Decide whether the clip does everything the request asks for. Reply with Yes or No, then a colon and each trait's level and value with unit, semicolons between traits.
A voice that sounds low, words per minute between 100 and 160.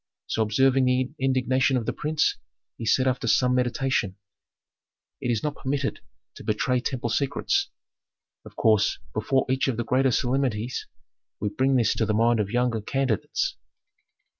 Yes: low, 125 Hz; average, 155 wpm